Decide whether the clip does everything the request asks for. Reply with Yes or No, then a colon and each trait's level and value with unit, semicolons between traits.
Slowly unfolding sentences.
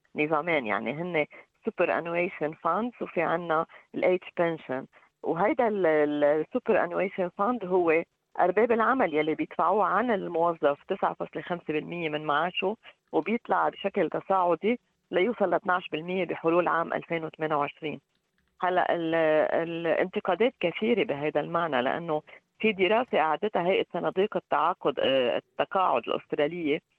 No: average, 105 wpm